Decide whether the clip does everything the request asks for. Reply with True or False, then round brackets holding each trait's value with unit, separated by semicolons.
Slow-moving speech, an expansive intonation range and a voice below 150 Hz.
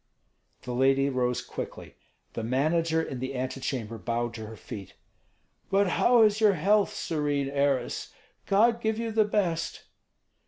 False (145 wpm; 8.1 semitones; 140 Hz)